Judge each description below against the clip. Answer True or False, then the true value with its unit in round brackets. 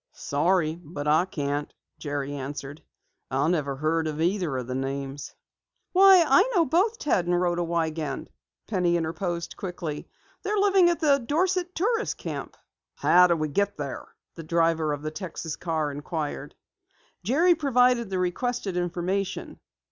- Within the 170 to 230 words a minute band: False (145 wpm)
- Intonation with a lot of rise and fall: True (8.4 semitones)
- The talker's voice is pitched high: False (175 Hz)